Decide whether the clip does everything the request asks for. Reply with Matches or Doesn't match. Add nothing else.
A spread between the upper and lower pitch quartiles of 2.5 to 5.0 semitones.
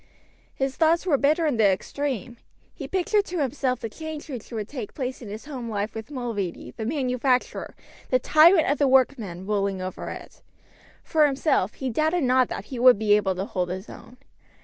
Doesn't match